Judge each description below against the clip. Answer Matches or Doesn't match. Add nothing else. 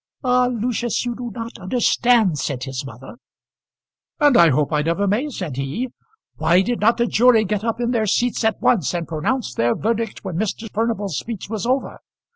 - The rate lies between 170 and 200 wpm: Matches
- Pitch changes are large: Matches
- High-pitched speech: Matches